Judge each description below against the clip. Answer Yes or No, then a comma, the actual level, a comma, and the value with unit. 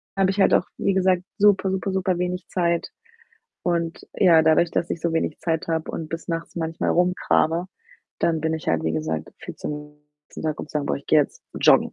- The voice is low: No, medium, 165 Hz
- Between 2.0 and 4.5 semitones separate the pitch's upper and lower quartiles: Yes, narrow, 2.6 semitones